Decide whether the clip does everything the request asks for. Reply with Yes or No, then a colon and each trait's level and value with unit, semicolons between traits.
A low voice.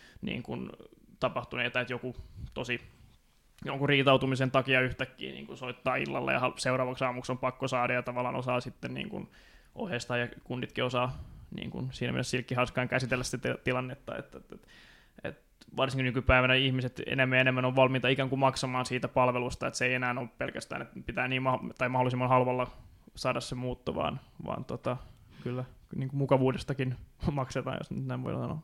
Yes: low, 125 Hz